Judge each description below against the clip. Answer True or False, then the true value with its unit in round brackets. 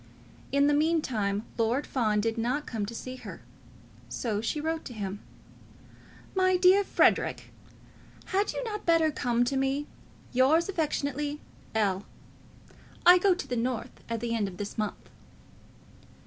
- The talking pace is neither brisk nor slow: True (150 wpm)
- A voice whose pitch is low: False (260 Hz)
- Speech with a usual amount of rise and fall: False (6.2 semitones)